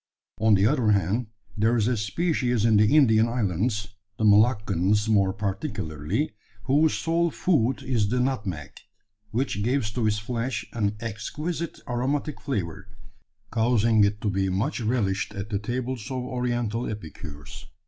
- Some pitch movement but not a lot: Yes, average, 3.6 semitones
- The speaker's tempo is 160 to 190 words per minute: No, average, 145 wpm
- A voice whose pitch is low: Yes, low, 110 Hz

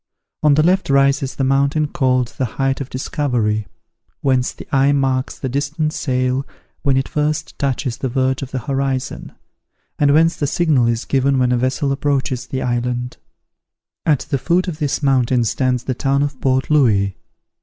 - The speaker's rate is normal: Yes, average, 175 wpm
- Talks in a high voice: No, low, 135 Hz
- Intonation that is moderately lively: No, narrow, 1.9 semitones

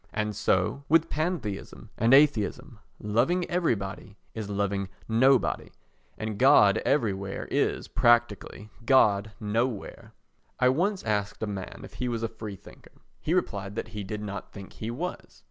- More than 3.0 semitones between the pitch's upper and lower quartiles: Yes, average, 4.4 semitones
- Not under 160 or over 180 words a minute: No, average, 145 wpm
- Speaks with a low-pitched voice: Yes, low, 110 Hz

